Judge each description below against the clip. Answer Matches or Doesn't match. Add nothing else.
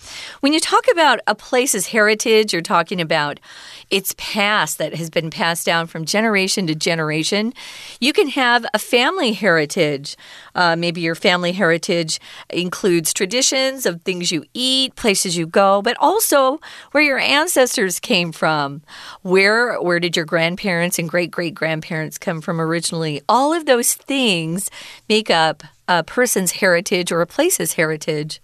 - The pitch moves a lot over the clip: Matches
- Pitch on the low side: Doesn't match